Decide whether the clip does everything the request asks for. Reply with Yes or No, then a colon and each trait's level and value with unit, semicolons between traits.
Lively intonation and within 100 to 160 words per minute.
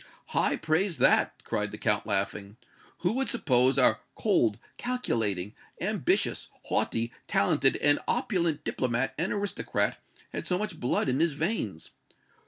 Yes: wide, 7.8 semitones; slow, 135 wpm